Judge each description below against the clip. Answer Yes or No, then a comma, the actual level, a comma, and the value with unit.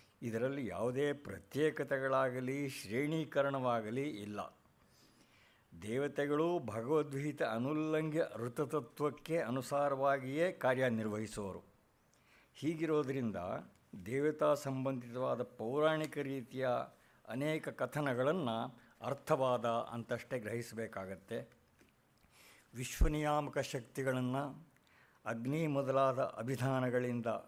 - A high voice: No, low, 135 Hz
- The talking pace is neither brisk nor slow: No, slow, 55 wpm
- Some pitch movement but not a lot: Yes, average, 3.7 semitones